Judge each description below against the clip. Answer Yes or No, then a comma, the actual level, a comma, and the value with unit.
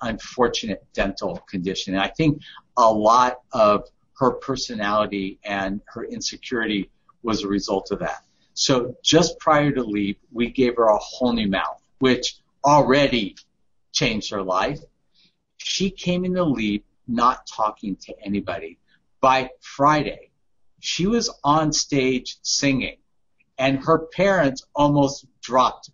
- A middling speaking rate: No, slow, 130 wpm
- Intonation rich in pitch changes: Yes, wide, 6.0 semitones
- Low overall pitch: Yes, low, 130 Hz